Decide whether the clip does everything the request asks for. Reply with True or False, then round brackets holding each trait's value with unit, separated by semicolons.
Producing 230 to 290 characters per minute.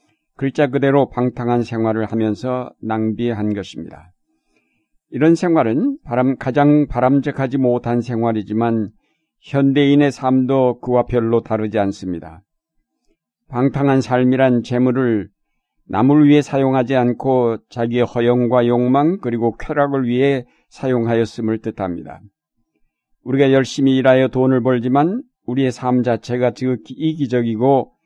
True (285 characters per minute)